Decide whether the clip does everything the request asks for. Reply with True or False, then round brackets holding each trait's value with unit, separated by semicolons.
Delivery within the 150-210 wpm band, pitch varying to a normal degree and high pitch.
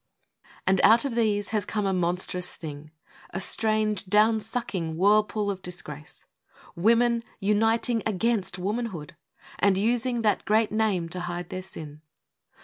False (140 wpm; 3.7 semitones; 205 Hz)